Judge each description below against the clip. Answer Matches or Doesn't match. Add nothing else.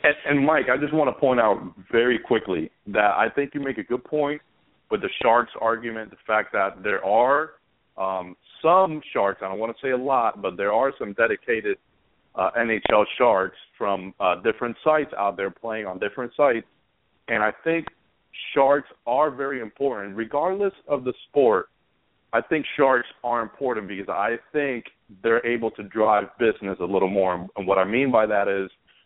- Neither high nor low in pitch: Doesn't match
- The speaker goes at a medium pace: Matches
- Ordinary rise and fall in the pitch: Doesn't match